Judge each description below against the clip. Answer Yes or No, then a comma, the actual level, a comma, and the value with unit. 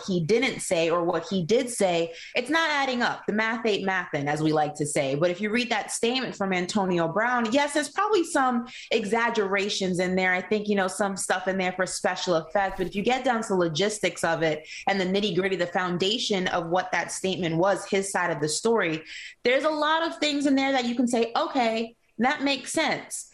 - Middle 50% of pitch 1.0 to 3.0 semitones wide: No, average, 5.0 semitones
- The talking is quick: Yes, fast, 225 wpm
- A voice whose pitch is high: Yes, high, 200 Hz